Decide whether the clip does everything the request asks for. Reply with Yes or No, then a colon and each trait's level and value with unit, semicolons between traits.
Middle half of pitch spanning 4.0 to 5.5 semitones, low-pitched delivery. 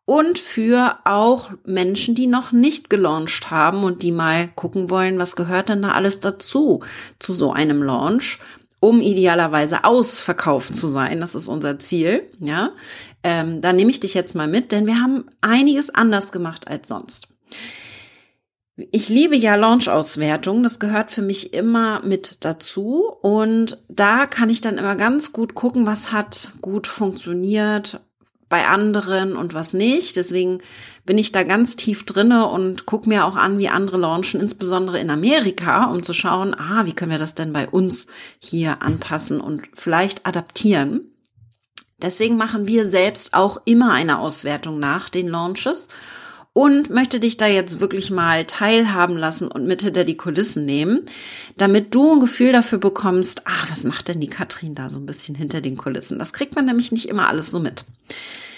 No: average, 4.8 semitones; high, 195 Hz